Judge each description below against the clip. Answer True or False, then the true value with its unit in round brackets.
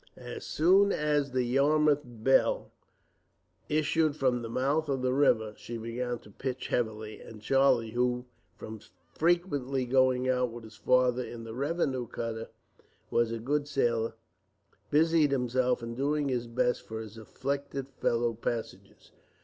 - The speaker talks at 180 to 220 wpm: False (145 wpm)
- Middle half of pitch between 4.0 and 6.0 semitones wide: False (3.3 semitones)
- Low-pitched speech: True (125 Hz)